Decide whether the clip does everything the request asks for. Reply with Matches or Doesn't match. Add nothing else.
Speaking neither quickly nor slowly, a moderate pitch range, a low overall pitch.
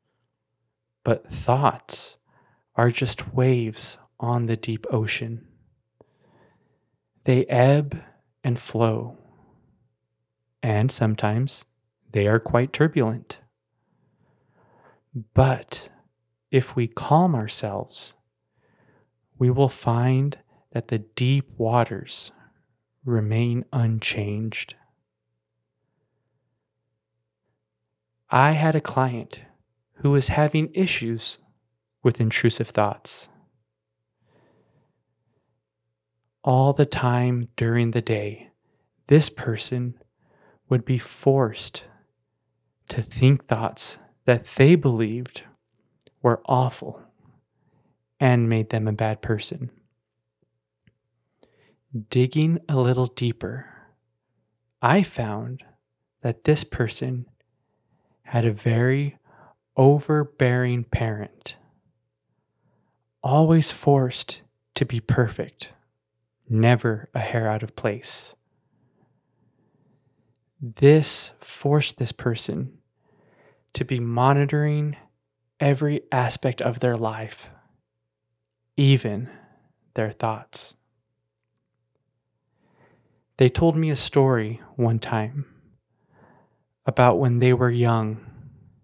Doesn't match